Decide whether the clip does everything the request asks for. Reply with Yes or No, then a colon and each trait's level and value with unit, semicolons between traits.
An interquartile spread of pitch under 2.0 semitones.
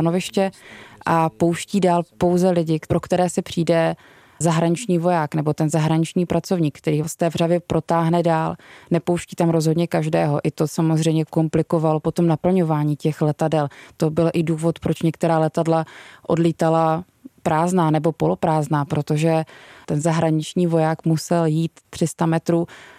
Yes: narrow, 1.3 semitones